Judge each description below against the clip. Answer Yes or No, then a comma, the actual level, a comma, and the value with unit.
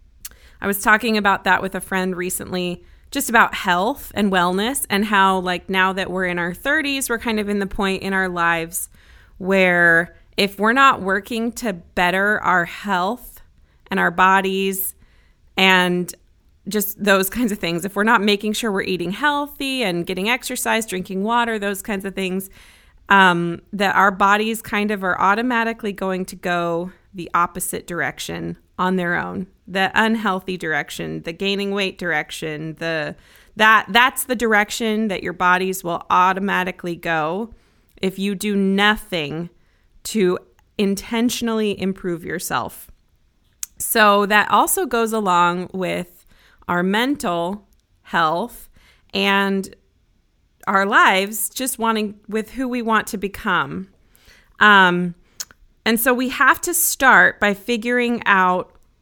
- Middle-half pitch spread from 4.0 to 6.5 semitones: No, average, 3.2 semitones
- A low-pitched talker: No, high, 195 Hz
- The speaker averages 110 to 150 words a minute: Yes, average, 140 wpm